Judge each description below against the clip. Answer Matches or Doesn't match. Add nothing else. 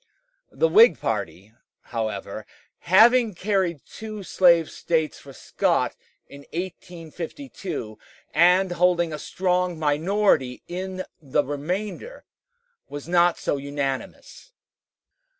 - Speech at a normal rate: Doesn't match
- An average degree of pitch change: Matches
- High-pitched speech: Doesn't match